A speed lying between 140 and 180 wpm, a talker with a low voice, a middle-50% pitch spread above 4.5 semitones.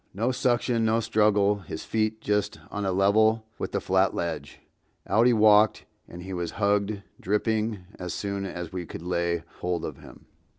No: average, 170 wpm; low, 100 Hz; average, 3.4 semitones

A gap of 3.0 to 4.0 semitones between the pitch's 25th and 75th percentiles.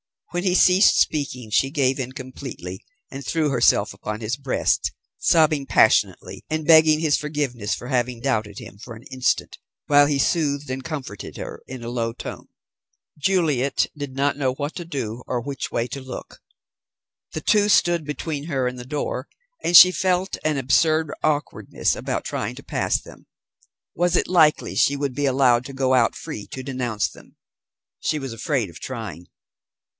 Yes: average, 3.7 semitones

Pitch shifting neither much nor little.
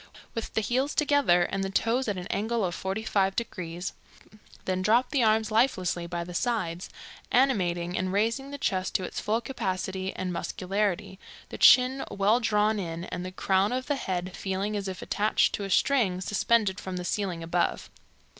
Yes: average, 3.8 semitones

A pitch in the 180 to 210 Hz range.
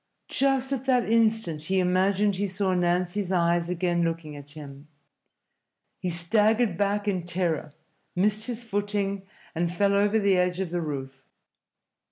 Yes: medium, 185 Hz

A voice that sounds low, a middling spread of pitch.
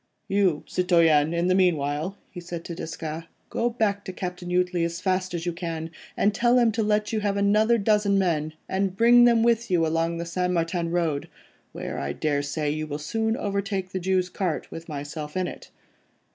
No: medium, 180 Hz; average, 3.5 semitones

